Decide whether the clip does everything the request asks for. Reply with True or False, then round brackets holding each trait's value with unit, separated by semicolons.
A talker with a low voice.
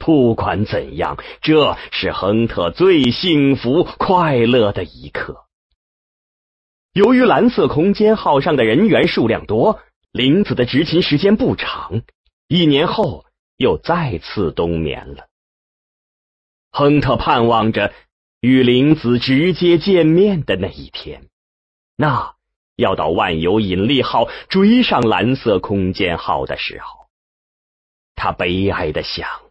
True (125 Hz)